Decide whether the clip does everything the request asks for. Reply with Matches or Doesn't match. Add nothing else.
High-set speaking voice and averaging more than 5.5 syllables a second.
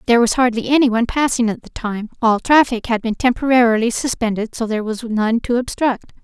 Matches